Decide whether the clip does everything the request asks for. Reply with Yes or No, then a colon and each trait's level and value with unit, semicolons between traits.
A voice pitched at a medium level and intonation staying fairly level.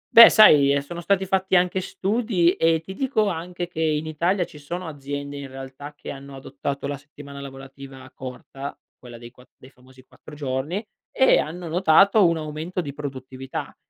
No: medium, 150 Hz; average, 4.6 semitones